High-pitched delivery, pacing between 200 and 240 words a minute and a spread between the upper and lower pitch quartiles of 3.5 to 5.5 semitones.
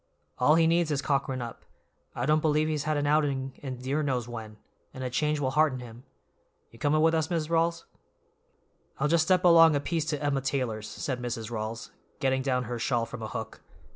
No: medium, 140 Hz; fast, 205 wpm; average, 3.9 semitones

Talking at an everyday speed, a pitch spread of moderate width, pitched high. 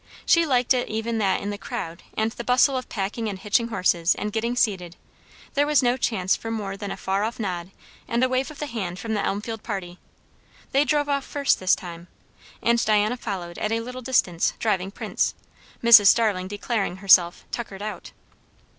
Yes: average, 190 wpm; average, 4.0 semitones; high, 215 Hz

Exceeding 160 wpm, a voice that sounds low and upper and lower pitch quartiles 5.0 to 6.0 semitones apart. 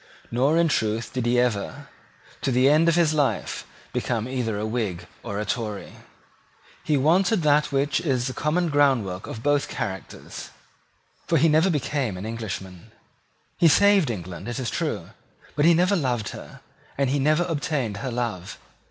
Yes: average, 170 wpm; low, 130 Hz; wide, 5.5 semitones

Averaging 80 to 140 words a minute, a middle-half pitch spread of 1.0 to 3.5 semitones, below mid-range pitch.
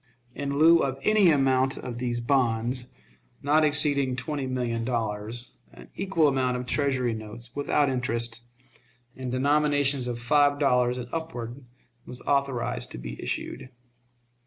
Yes: slow, 135 wpm; average, 3.1 semitones; low, 130 Hz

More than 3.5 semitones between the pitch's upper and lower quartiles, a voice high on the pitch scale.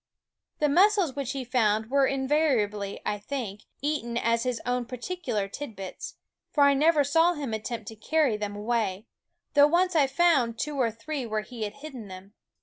Yes: average, 5.1 semitones; very high, 250 Hz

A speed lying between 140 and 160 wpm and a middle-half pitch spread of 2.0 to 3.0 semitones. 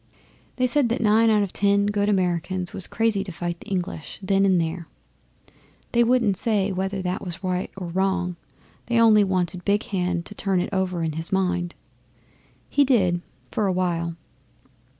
No: average, 175 wpm; narrow, 2.6 semitones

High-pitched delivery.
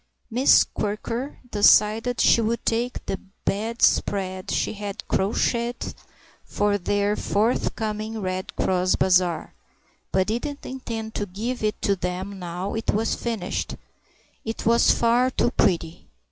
Yes: high, 210 Hz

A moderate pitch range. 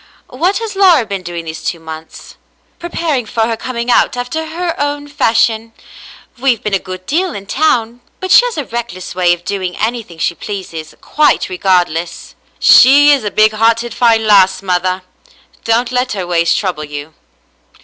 No: wide, 6.3 semitones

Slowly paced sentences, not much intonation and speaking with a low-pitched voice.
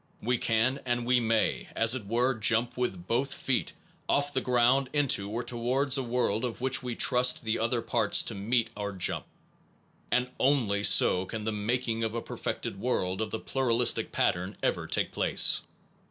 No: average, 185 wpm; narrow, 2.3 semitones; low, 120 Hz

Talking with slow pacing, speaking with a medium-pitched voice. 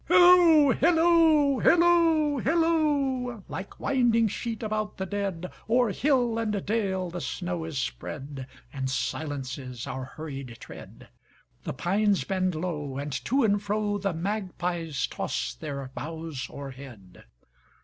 No: slow, 110 wpm; high, 195 Hz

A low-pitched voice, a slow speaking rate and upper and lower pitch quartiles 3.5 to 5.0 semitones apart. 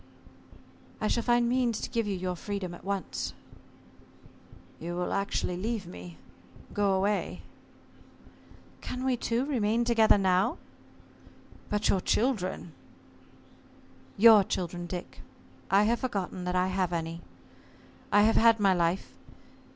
No: high, 200 Hz; slow, 130 wpm; average, 4.0 semitones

